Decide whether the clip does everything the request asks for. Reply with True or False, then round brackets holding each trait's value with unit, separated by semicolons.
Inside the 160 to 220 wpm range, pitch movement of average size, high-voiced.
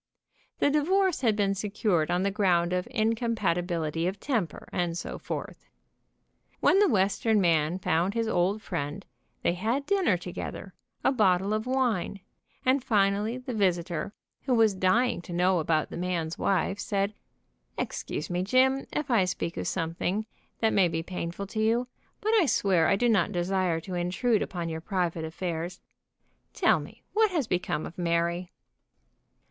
True (165 wpm; 4.5 semitones; 195 Hz)